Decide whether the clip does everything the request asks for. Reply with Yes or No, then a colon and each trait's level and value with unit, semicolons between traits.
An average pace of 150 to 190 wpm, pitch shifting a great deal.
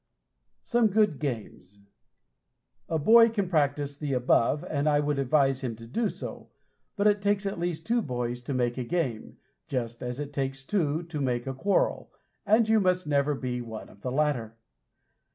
Yes: average, 180 wpm; wide, 6.5 semitones